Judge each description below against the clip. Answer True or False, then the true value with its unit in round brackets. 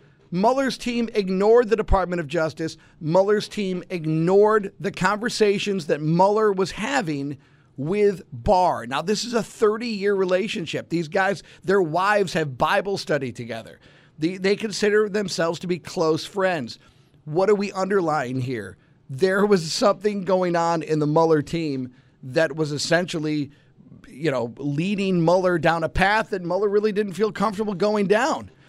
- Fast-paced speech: False (150 wpm)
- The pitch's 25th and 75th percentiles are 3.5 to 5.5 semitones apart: True (4.9 semitones)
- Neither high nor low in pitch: True (180 Hz)